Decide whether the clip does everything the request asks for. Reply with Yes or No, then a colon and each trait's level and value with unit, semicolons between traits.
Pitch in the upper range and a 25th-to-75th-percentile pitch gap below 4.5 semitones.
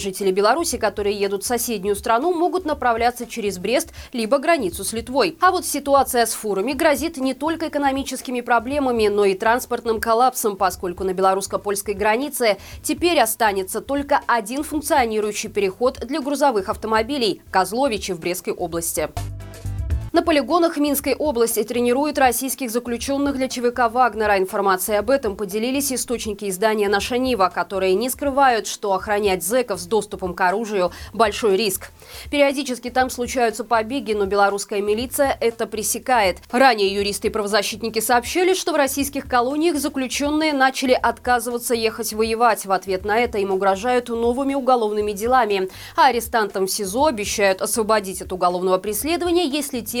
No: high, 235 Hz; average, 4.9 semitones